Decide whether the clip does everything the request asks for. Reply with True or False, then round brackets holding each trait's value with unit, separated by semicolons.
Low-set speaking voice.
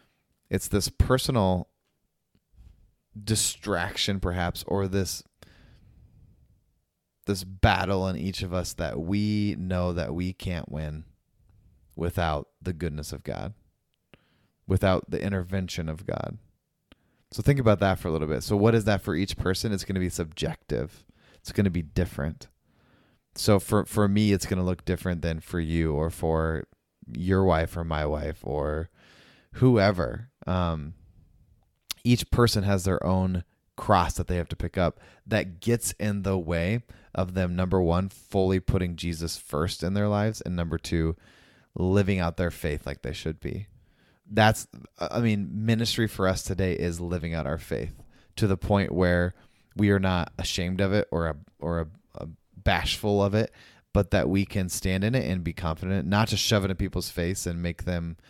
True (95 Hz)